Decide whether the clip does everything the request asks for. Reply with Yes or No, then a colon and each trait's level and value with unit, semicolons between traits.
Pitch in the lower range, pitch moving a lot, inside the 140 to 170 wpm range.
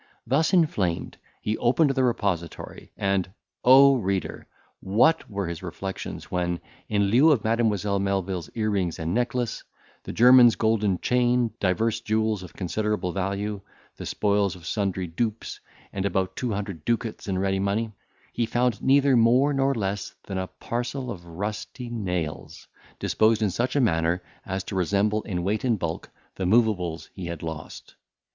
No: low, 105 Hz; average, 4.1 semitones; average, 155 wpm